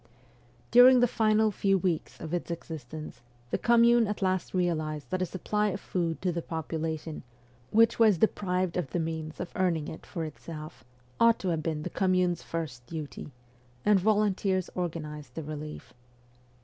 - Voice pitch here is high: No, medium, 175 Hz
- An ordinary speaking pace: Yes, average, 170 wpm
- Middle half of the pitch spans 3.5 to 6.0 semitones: Yes, average, 4.0 semitones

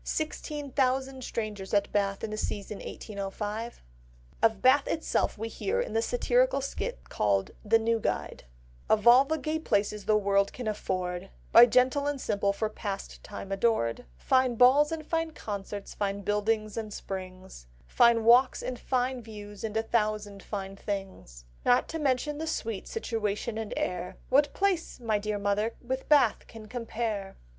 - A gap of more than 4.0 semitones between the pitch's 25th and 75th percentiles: Yes, average, 4.4 semitones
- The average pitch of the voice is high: Yes, high, 220 Hz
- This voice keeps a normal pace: Yes, average, 160 wpm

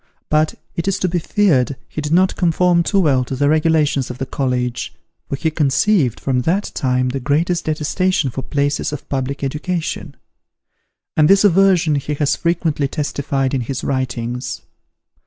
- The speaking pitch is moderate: Yes, medium, 150 Hz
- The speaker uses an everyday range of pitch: Yes, average, 4.2 semitones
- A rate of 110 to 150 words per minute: No, average, 165 wpm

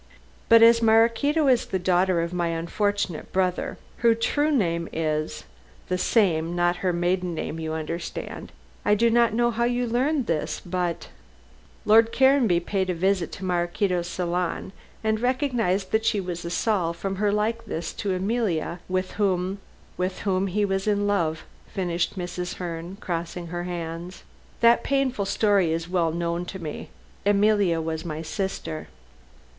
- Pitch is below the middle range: No, medium, 185 Hz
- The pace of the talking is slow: No, average, 160 wpm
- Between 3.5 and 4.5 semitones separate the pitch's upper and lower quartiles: Yes, average, 4.1 semitones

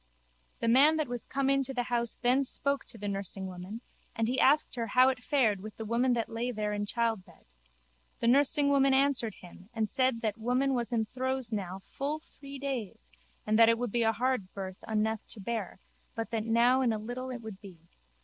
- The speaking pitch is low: No, high, 235 Hz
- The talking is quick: Yes, fast, 215 wpm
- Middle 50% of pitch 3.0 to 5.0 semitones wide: Yes, average, 3.3 semitones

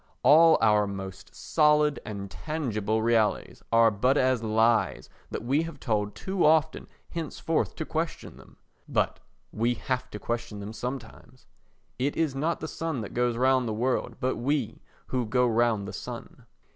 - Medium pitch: No, low, 125 Hz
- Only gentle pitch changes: No, average, 5.2 semitones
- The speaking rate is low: No, average, 160 wpm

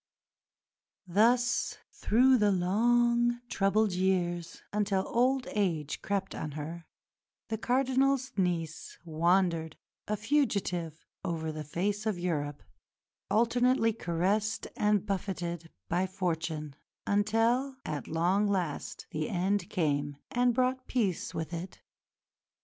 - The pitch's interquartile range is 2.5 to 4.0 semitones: No, average, 5.1 semitones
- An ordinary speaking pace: No, slow, 110 wpm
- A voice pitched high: Yes, high, 195 Hz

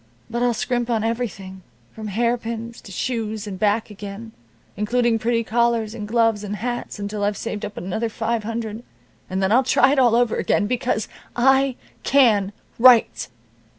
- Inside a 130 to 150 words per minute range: No, average, 165 wpm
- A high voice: Yes, high, 225 Hz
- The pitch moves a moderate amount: No, narrow, 2.3 semitones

